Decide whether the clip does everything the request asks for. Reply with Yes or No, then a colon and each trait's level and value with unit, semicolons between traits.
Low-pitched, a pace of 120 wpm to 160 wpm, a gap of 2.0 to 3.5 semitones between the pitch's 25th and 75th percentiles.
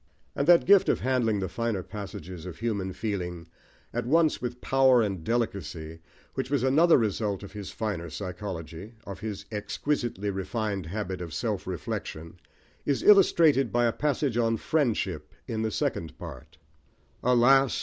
No: low, 110 Hz; average, 150 wpm; average, 5.1 semitones